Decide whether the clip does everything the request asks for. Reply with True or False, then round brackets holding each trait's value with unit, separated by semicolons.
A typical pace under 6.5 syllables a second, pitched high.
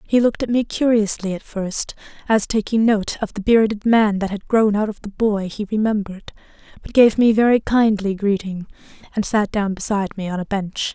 True (5.4 syllables/s; 210 Hz)